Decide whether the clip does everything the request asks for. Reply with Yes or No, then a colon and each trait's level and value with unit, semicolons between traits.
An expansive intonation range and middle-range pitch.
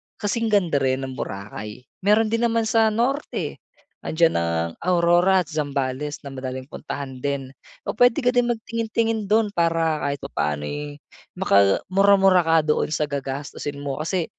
Yes: wide, 7.6 semitones; medium, 160 Hz